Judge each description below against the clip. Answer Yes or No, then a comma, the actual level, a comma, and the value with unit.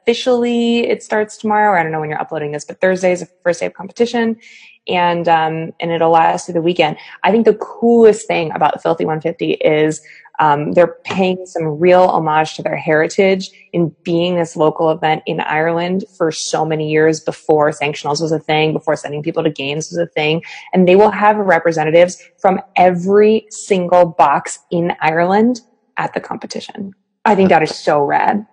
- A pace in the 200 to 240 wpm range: No, average, 185 wpm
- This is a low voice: No, medium, 175 Hz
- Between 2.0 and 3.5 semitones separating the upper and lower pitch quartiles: No, average, 4.2 semitones